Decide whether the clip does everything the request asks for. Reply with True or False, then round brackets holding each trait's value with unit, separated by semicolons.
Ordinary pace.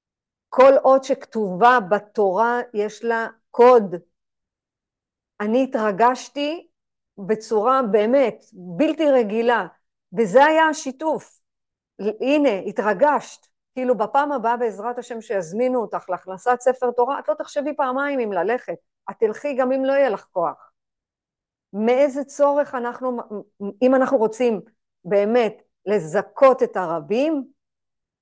True (110 wpm)